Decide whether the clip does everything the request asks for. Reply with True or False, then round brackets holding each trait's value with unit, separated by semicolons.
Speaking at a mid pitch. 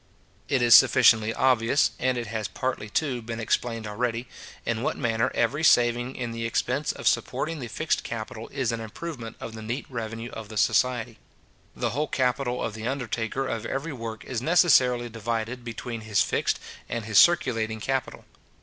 False (120 Hz)